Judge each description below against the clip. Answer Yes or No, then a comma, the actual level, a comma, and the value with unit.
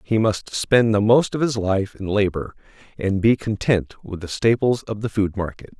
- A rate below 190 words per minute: No, fast, 205 wpm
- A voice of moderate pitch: No, low, 105 Hz